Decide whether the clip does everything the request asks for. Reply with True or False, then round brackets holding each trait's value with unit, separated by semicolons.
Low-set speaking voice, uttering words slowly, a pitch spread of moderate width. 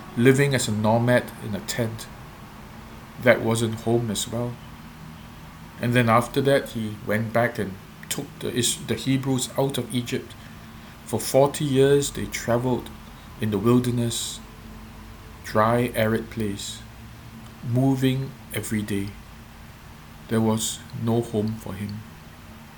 False (115 Hz; 125 wpm; 2.0 semitones)